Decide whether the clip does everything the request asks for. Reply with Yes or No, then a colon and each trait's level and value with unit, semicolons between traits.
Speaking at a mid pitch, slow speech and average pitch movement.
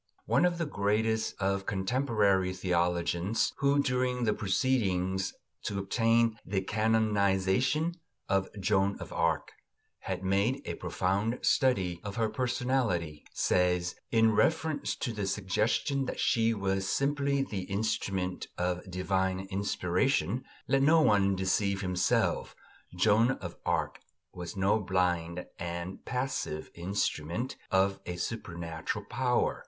No: low, 100 Hz; slow, 120 wpm; average, 4.2 semitones